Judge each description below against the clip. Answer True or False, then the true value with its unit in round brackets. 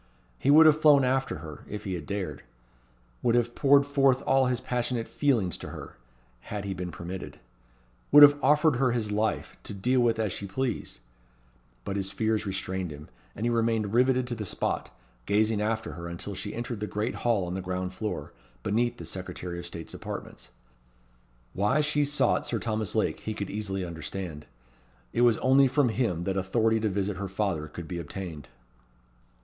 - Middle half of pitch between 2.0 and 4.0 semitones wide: False (4.7 semitones)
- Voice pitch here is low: True (105 Hz)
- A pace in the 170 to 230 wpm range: True (185 wpm)